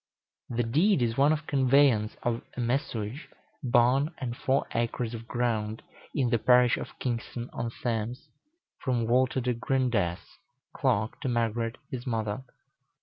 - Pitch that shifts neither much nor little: No, narrow, 2.3 semitones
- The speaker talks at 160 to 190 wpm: No, average, 145 wpm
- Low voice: Yes, low, 120 Hz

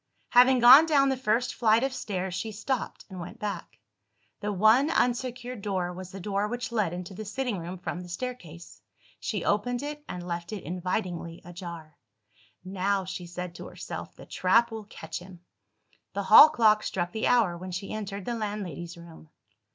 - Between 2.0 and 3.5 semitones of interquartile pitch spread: No, average, 4.8 semitones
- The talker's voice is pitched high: Yes, high, 200 Hz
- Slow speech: No, average, 180 wpm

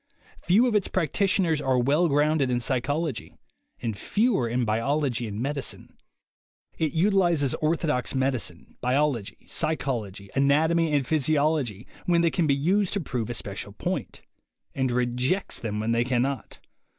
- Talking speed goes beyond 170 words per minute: No, average, 145 wpm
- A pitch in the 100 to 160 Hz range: Yes, medium, 140 Hz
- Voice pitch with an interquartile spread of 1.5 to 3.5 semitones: No, average, 4.8 semitones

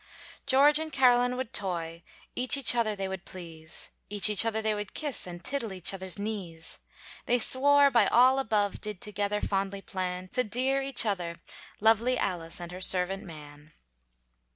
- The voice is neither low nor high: No, high, 205 Hz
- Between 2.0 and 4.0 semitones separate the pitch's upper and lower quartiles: No, average, 5.3 semitones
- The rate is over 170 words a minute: No, average, 160 wpm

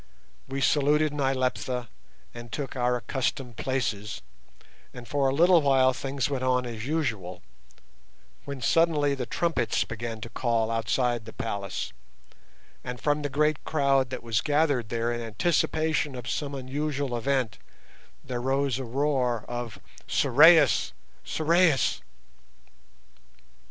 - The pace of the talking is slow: Yes, slow, 125 wpm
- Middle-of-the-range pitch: No, low, 130 Hz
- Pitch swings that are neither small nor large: Yes, average, 3.4 semitones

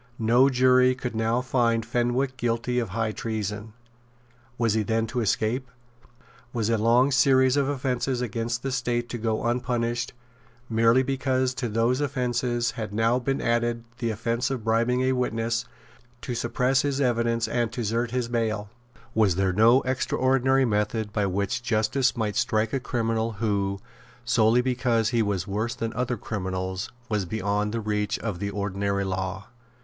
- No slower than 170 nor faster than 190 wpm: No, average, 160 wpm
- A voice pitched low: Yes, low, 115 Hz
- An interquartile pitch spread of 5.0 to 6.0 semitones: No, narrow, 2.5 semitones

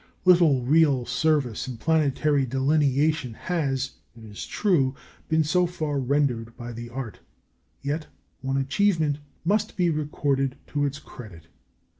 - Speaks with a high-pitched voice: No, medium, 140 Hz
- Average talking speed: No, slow, 130 wpm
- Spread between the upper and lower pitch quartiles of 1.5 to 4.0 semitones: Yes, average, 3.5 semitones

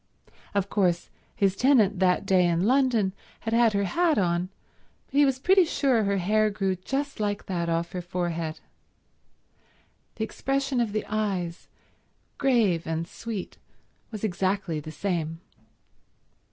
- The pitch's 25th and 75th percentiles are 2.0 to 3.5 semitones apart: No, average, 4.8 semitones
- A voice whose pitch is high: Yes, high, 200 Hz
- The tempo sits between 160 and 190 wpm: No, average, 140 wpm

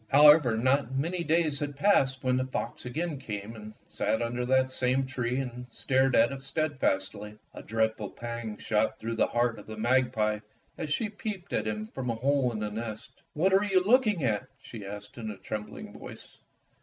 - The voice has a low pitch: Yes, low, 125 Hz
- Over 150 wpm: Yes, average, 200 wpm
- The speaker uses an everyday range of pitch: Yes, average, 4.3 semitones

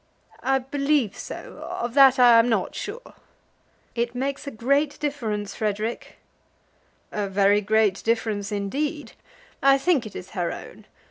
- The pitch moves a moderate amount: Yes, average, 4.9 semitones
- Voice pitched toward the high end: Yes, high, 235 Hz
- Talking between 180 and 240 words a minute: No, average, 140 wpm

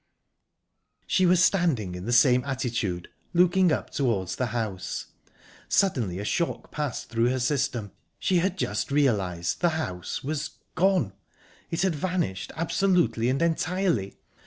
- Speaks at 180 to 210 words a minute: No, slow, 135 wpm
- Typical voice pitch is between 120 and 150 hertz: Yes, low, 135 Hz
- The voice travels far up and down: Yes, wide, 8.3 semitones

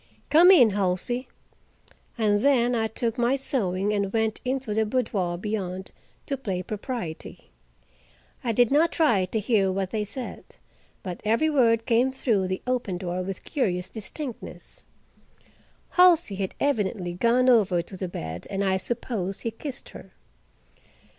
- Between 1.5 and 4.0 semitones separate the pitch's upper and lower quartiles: No, average, 4.9 semitones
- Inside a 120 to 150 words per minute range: Yes, average, 145 wpm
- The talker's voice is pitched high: Yes, high, 220 Hz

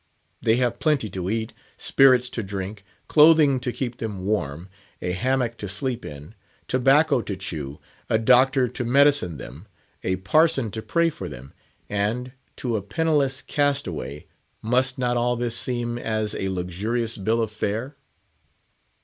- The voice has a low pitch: Yes, low, 115 Hz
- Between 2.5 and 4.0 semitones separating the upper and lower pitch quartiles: No, average, 4.8 semitones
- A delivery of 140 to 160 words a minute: Yes, average, 150 wpm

